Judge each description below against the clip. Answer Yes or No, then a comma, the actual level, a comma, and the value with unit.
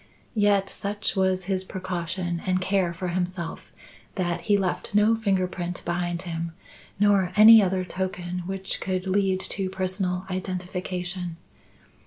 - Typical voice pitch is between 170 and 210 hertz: Yes, medium, 185 Hz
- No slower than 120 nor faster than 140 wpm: Yes, slow, 135 wpm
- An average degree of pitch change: No, narrow, 1.4 semitones